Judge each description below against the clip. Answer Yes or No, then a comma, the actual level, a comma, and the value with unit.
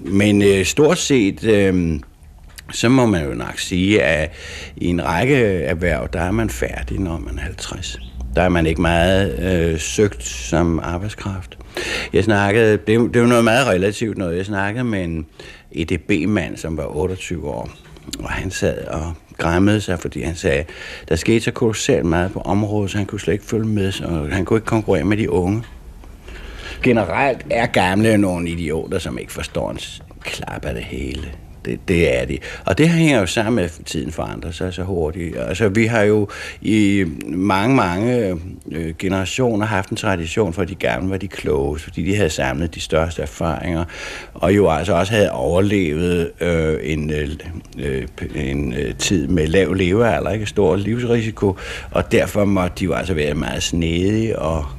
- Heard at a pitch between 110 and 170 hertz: No, very low, 90 Hz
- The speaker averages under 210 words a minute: Yes, average, 180 wpm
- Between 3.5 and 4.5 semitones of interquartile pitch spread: Yes, average, 4.1 semitones